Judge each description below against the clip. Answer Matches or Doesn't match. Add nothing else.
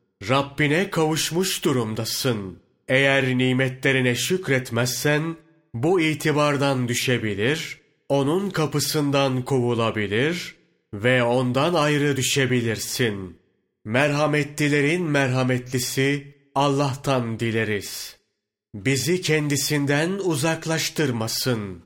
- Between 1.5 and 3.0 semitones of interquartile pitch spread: Doesn't match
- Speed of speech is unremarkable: Doesn't match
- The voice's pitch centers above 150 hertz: Doesn't match